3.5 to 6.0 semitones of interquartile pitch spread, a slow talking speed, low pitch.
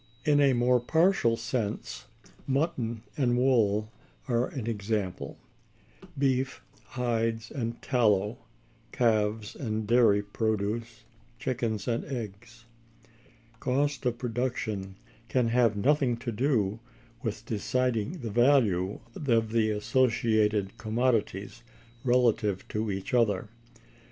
No: average, 2.9 semitones; slow, 105 wpm; low, 115 Hz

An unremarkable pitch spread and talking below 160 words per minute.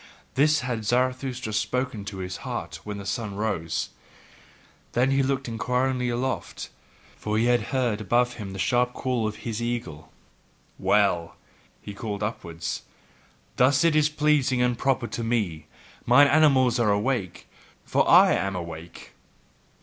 Yes: average, 4.0 semitones; average, 140 wpm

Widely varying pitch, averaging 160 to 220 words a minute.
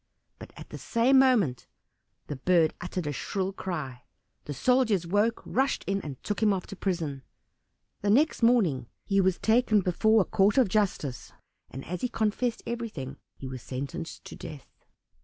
Yes: wide, 6.7 semitones; average, 165 wpm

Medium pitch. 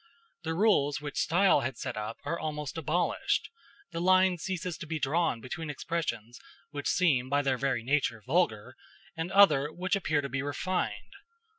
Yes: medium, 150 Hz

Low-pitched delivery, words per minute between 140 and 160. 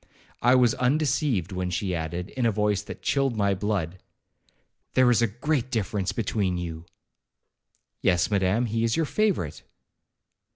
Yes: low, 105 Hz; average, 150 wpm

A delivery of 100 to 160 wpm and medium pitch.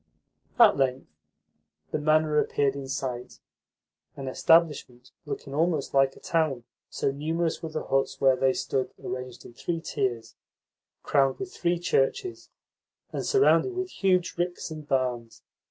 Yes: average, 140 wpm; medium, 145 Hz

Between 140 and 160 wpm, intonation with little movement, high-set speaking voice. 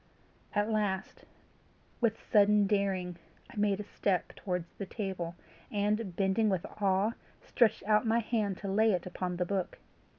Yes: average, 155 wpm; narrow, 2.2 semitones; high, 200 Hz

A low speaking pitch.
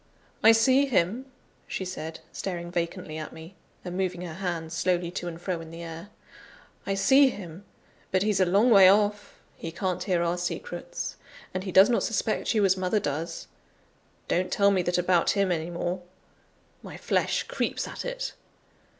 No: medium, 185 Hz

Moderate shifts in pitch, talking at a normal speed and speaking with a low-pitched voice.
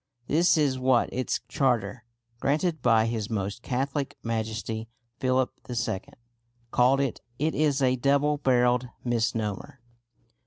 No: average, 3.4 semitones; slow, 120 wpm; low, 125 Hz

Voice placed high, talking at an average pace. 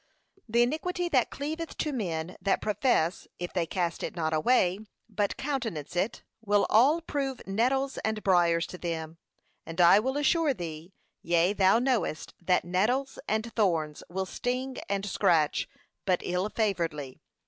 Yes: high, 200 Hz; average, 150 wpm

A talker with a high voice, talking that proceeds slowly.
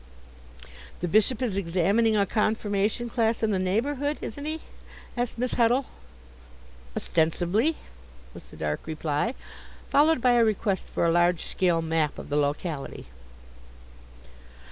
Yes: high, 210 Hz; slow, 130 wpm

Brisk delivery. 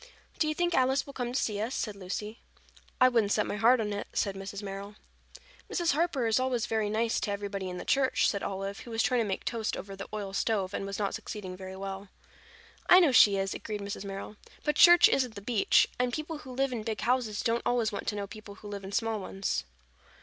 Yes: fast, 235 wpm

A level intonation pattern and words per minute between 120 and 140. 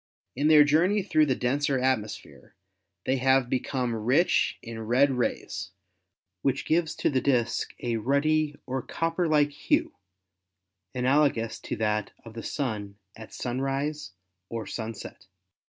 No: average, 4.2 semitones; slow, 135 wpm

